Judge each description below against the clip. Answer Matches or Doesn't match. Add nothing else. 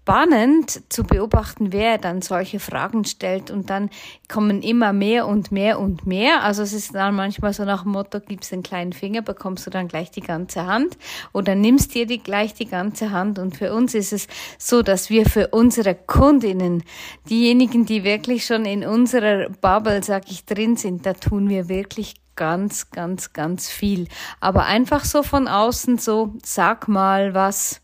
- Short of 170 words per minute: Doesn't match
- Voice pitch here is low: Doesn't match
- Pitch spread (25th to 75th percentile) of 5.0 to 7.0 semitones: Doesn't match